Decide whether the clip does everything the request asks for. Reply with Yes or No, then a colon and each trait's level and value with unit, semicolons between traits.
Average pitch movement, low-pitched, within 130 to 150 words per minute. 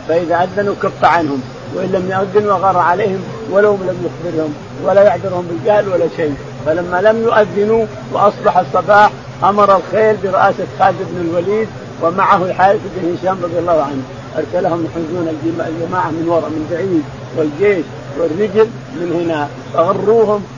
No: average, 3.6 semitones; medium, 175 Hz; fast, 135 wpm